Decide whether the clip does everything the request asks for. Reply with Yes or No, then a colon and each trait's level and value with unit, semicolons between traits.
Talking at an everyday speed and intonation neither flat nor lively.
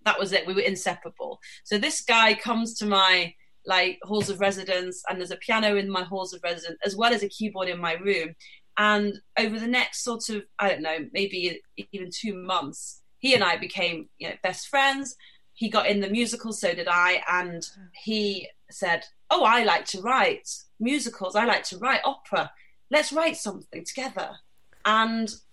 Yes: average, 190 wpm; average, 3.6 semitones